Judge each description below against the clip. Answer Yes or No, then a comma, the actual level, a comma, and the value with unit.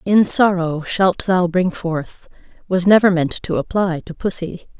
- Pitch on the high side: No, medium, 180 Hz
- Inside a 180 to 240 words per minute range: No, average, 165 wpm